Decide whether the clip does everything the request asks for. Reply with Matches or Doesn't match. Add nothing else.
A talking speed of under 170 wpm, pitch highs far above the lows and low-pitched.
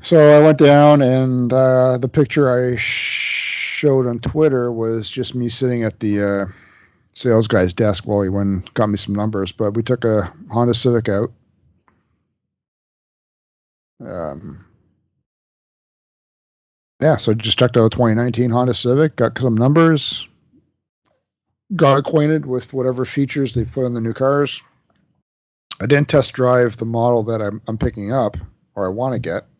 Doesn't match